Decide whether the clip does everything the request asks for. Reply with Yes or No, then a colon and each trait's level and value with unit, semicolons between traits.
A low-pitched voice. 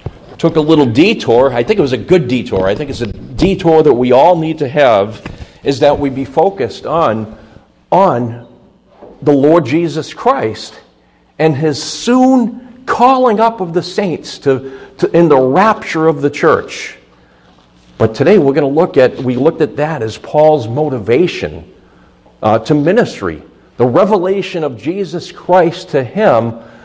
No: medium, 150 Hz